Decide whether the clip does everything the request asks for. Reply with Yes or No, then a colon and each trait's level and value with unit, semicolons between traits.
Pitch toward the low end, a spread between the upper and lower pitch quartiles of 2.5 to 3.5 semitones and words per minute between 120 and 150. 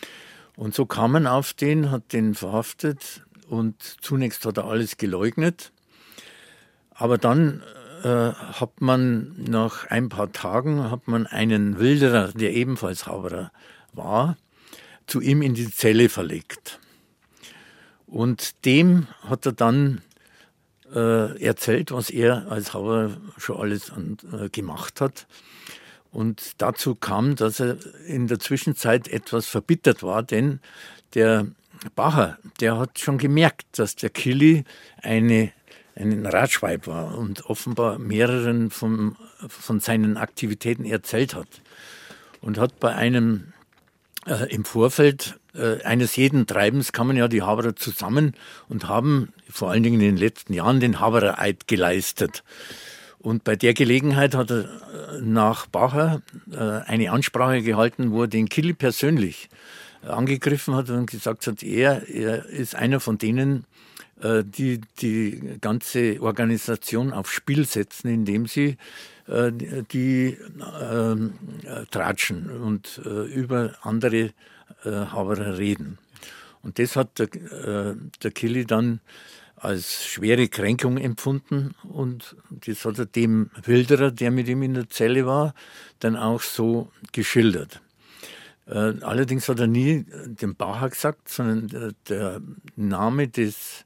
Yes: low, 115 Hz; average, 3.1 semitones; average, 130 wpm